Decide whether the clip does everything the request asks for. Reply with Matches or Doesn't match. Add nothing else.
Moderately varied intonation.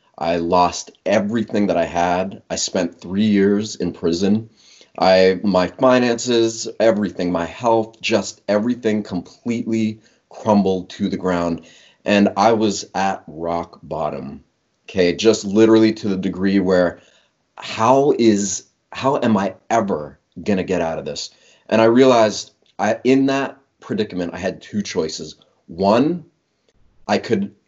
Matches